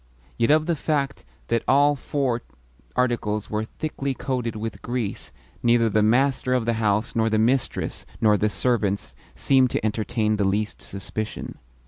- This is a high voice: No, low, 115 Hz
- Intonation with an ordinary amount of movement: Yes, average, 3.4 semitones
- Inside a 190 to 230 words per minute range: No, average, 155 wpm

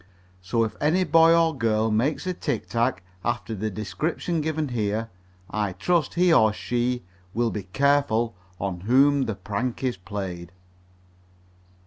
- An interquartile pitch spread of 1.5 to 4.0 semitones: No, average, 5.3 semitones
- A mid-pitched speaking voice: No, low, 120 Hz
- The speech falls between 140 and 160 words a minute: Yes, average, 145 wpm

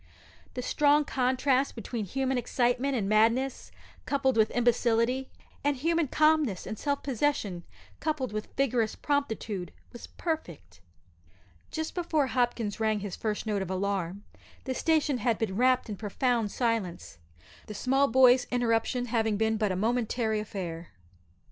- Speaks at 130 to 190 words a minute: Yes, average, 140 wpm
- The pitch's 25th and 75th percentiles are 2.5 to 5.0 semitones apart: Yes, average, 3.9 semitones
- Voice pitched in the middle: No, high, 240 Hz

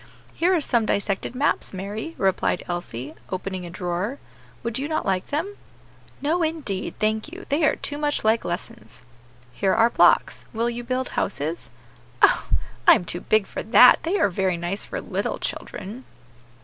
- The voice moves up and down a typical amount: No, wide, 7.4 semitones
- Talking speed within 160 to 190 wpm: Yes, average, 170 wpm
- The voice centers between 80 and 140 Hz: No, high, 215 Hz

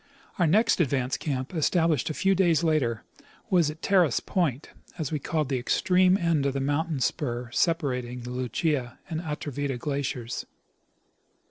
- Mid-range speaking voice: Yes, medium, 150 Hz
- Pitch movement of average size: Yes, average, 4.6 semitones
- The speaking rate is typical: Yes, average, 155 wpm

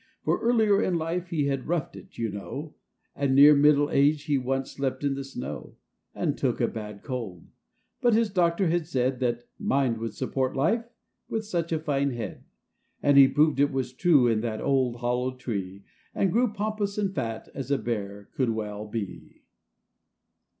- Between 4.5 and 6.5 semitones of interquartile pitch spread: Yes, wide, 5.5 semitones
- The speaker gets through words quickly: No, average, 180 wpm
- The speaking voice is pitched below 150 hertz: Yes, low, 135 Hz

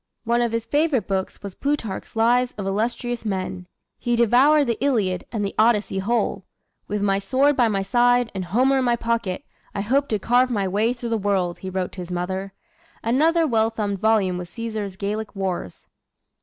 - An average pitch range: Yes, average, 3.8 semitones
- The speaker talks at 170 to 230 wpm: Yes, average, 190 wpm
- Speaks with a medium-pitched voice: No, high, 220 Hz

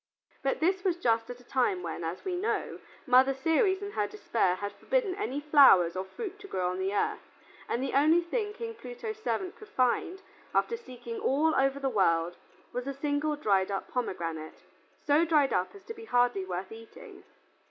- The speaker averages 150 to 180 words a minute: No, average, 195 wpm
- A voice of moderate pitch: No, very high, 270 Hz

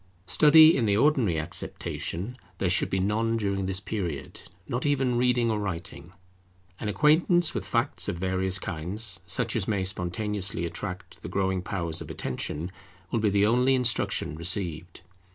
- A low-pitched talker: Yes, low, 100 Hz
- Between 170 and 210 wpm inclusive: No, average, 155 wpm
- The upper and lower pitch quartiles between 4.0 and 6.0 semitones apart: Yes, average, 4.6 semitones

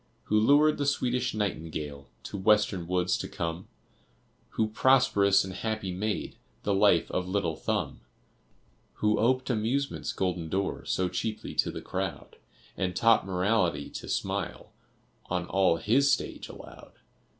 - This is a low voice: Yes, low, 100 Hz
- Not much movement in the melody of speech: No, average, 3.7 semitones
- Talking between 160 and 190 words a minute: No, average, 140 wpm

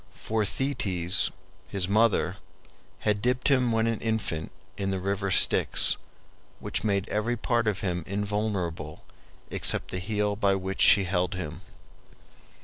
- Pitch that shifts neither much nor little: Yes, average, 3.0 semitones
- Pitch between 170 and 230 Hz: No, low, 100 Hz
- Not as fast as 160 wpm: Yes, average, 140 wpm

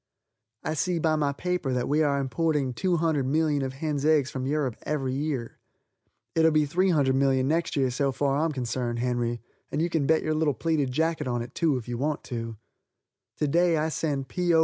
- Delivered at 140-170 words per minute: No, average, 200 wpm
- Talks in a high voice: No, medium, 145 Hz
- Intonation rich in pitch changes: No, average, 3.4 semitones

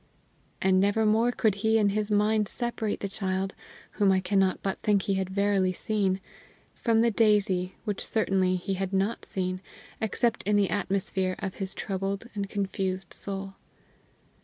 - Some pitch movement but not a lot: No, narrow, 1.8 semitones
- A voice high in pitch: Yes, high, 195 Hz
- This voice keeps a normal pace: Yes, average, 160 wpm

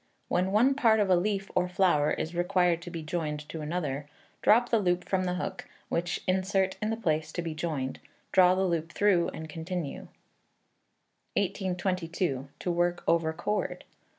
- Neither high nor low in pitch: Yes, medium, 180 Hz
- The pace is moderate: Yes, average, 170 wpm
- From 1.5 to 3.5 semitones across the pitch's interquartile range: Yes, average, 2.8 semitones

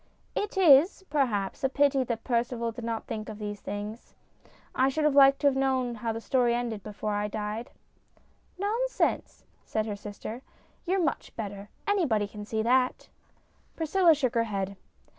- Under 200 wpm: Yes, average, 180 wpm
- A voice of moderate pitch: No, high, 235 Hz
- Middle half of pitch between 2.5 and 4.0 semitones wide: No, average, 4.6 semitones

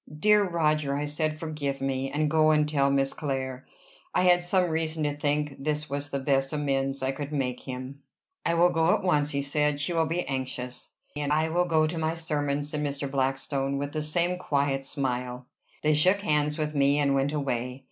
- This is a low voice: No, medium, 145 Hz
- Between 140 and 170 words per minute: No, average, 200 wpm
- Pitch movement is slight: Yes, narrow, 2.2 semitones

